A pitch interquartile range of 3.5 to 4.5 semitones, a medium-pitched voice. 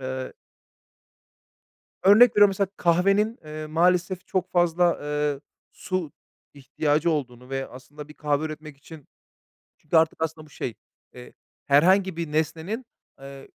Yes: average, 3.8 semitones; medium, 155 Hz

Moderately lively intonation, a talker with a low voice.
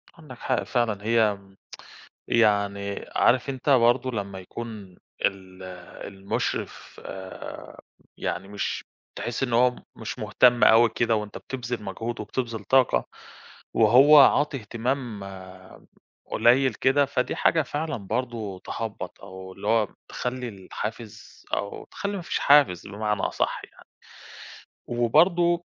Yes: average, 4.0 semitones; low, 115 Hz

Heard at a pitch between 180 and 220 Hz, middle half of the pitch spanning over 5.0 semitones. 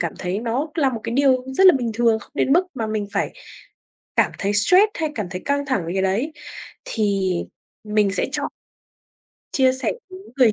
No: high, 235 Hz; wide, 5.5 semitones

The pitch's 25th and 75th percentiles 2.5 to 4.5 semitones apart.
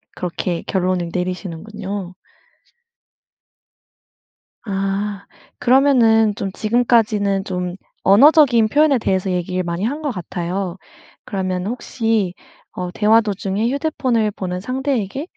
Yes: average, 4.1 semitones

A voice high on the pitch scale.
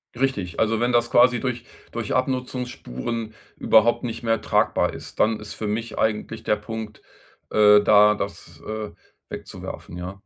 No: low, 110 Hz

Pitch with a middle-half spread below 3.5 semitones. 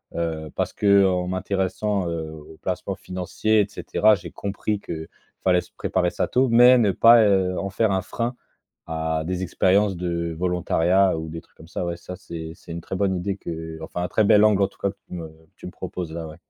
Yes: average, 3.1 semitones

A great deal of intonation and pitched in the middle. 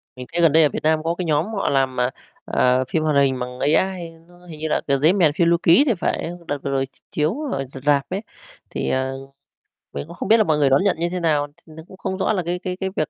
No: average, 4.1 semitones; medium, 160 Hz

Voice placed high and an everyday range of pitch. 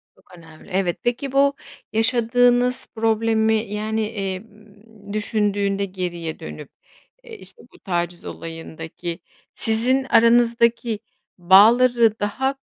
Yes: high, 220 Hz; average, 3.7 semitones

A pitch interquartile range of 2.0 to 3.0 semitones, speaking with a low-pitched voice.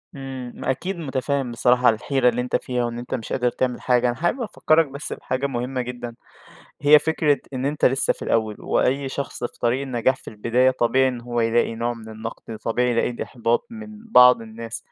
Yes: narrow, 2.4 semitones; low, 125 Hz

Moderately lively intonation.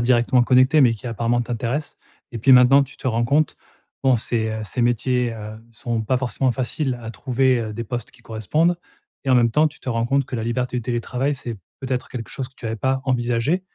No: narrow, 2.1 semitones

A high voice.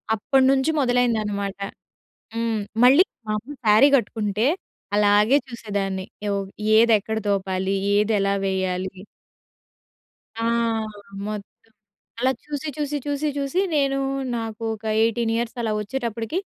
Yes: high, 225 Hz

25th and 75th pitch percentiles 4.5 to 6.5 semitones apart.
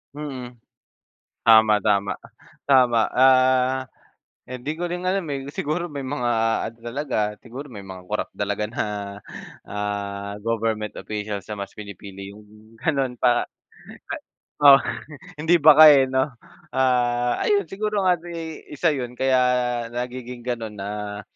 Yes: average, 5.1 semitones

